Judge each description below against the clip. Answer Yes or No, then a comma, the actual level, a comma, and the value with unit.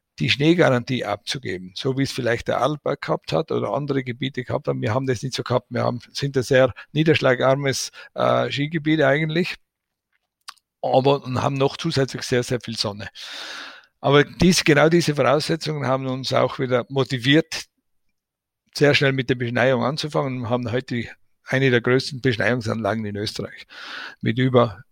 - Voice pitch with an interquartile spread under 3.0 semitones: Yes, narrow, 2.6 semitones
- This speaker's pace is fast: No, average, 160 wpm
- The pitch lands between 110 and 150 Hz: Yes, low, 130 Hz